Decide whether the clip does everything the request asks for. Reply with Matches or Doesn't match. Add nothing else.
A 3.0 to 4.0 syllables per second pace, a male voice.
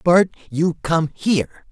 Matches